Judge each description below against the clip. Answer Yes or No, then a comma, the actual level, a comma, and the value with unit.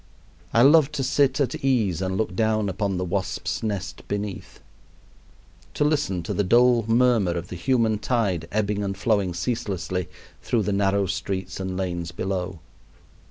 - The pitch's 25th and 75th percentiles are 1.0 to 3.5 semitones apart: No, average, 3.9 semitones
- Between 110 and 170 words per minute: Yes, average, 160 wpm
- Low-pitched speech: Yes, low, 100 Hz